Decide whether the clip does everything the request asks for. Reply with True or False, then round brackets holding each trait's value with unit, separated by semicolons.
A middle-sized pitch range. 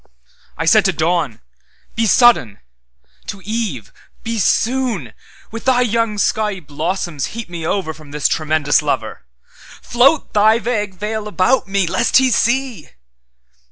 False (6.7 semitones)